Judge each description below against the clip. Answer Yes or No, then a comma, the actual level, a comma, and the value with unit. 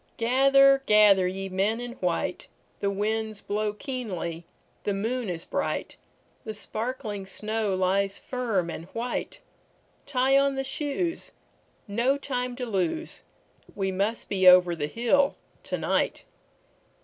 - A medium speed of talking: No, slow, 115 wpm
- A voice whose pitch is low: No, high, 215 Hz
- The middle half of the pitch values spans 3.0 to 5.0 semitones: Yes, average, 4.7 semitones